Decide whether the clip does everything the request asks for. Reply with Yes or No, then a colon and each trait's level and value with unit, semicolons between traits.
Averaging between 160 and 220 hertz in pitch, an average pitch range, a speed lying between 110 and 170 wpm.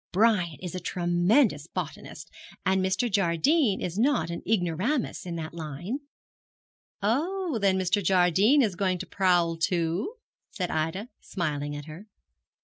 Yes: medium, 185 Hz; average, 4.2 semitones; average, 140 wpm